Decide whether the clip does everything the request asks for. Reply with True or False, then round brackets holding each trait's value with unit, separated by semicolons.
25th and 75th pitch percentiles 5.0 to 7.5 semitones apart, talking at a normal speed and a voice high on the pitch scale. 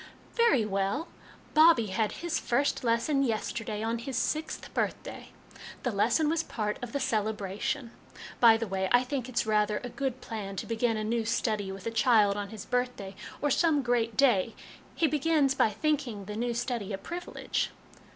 False (4.4 semitones; 180 wpm; 230 Hz)